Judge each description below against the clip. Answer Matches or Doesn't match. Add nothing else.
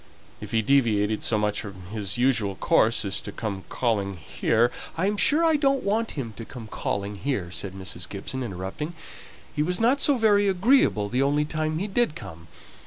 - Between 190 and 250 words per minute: Matches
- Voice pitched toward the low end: Matches